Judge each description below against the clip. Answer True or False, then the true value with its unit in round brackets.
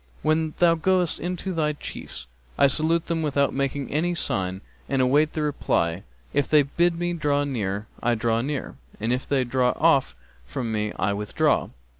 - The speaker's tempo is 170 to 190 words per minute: True (175 wpm)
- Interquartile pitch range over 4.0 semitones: True (5.1 semitones)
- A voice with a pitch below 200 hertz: True (140 Hz)